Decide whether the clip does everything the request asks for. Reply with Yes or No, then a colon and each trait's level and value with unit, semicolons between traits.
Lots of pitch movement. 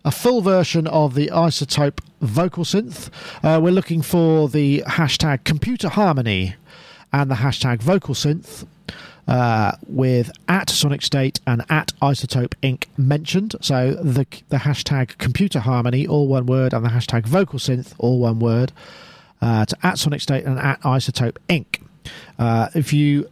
No: average, 4.1 semitones